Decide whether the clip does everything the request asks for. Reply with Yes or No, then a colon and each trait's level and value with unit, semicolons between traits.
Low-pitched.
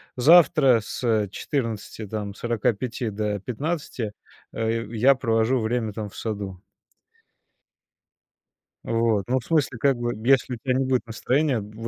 Yes: low, 115 Hz